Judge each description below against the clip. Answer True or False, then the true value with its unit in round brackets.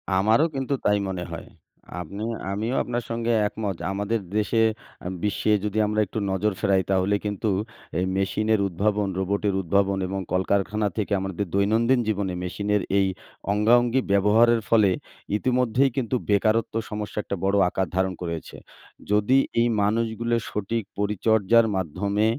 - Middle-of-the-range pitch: False (105 Hz)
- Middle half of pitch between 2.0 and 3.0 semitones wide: True (2.5 semitones)